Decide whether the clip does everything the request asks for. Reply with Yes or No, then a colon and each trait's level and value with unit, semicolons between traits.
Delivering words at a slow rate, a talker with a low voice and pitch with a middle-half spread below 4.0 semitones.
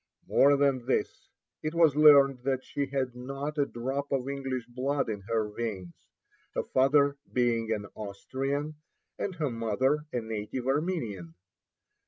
No: average, 145 wpm; low, 130 Hz; average, 3.6 semitones